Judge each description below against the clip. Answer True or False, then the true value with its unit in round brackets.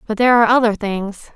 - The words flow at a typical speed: False (220 wpm)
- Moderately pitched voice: False (220 Hz)